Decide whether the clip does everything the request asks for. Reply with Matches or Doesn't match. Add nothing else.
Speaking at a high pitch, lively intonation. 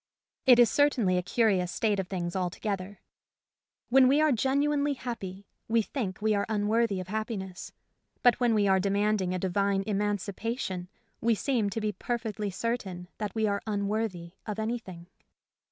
Doesn't match